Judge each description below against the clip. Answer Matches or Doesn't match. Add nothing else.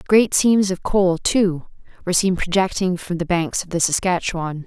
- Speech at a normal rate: Matches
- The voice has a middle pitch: Matches